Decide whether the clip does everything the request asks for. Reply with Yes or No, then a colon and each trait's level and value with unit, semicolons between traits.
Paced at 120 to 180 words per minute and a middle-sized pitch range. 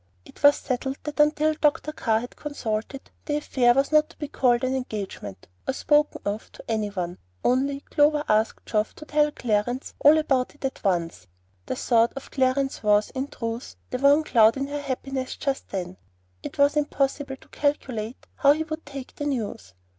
No: average, 190 wpm; average, 4.5 semitones